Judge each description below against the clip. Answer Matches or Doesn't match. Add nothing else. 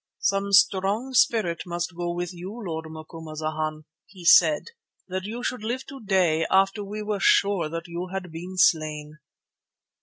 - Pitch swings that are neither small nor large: Matches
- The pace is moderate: Matches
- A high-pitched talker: Doesn't match